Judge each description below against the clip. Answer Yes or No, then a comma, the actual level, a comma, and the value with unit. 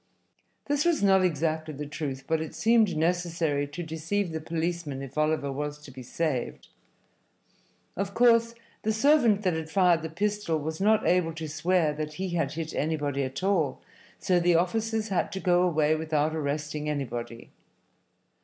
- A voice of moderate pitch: Yes, medium, 160 Hz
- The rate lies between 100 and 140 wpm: No, average, 165 wpm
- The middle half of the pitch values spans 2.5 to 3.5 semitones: No, average, 4.0 semitones